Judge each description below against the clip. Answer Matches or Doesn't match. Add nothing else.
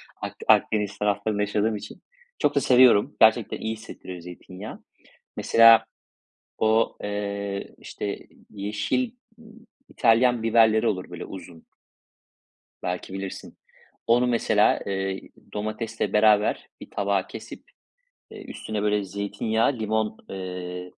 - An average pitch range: Doesn't match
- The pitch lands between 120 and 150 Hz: Doesn't match